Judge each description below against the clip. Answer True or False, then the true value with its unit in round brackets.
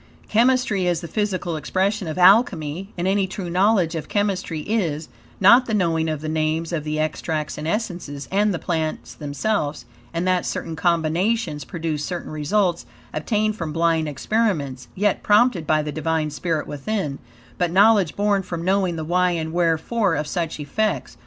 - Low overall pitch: False (170 Hz)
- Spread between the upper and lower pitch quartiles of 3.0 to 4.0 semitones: False (4.4 semitones)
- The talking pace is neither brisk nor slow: True (165 wpm)